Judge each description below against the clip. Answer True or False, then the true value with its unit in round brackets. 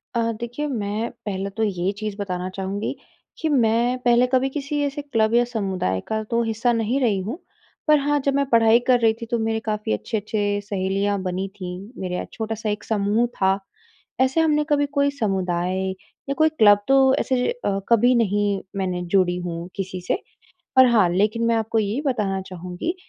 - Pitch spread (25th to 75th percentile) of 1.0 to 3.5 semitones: False (4.2 semitones)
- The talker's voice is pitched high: True (220 Hz)